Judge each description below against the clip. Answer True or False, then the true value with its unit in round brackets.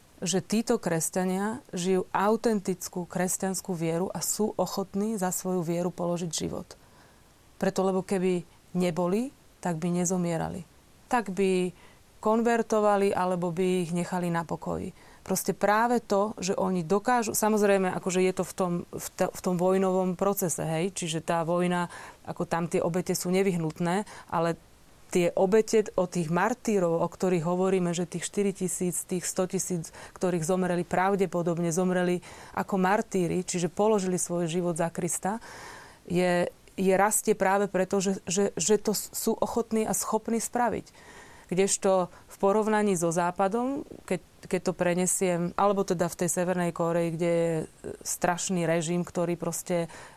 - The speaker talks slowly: False (145 wpm)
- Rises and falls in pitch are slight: True (2.1 semitones)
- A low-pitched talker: False (185 Hz)